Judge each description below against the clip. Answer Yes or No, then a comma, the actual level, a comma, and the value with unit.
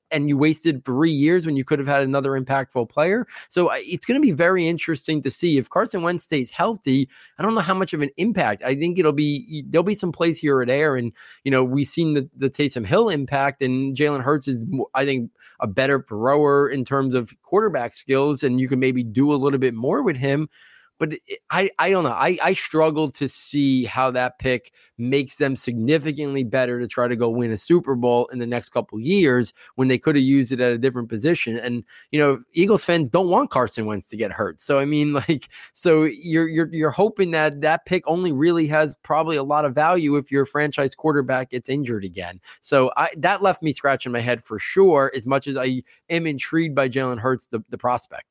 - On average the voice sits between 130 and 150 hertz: Yes, medium, 140 Hz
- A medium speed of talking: No, fast, 225 wpm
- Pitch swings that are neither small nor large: Yes, average, 3.8 semitones